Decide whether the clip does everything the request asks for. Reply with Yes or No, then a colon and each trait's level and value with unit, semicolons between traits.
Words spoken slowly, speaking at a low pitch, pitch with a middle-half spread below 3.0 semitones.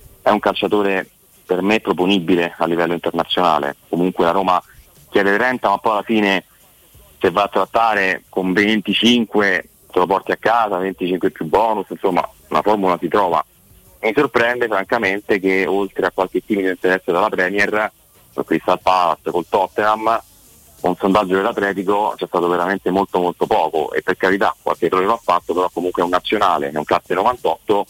No: fast, 170 wpm; very low, 95 Hz; narrow, 2.4 semitones